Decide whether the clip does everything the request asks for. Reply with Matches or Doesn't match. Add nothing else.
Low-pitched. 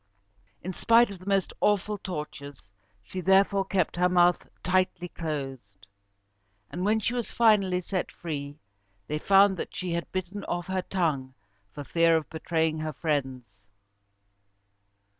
Doesn't match